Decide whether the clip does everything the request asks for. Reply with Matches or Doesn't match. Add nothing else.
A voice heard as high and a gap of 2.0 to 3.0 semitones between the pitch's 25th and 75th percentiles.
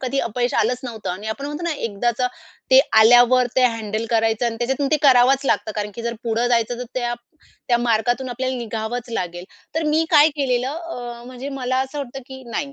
Matches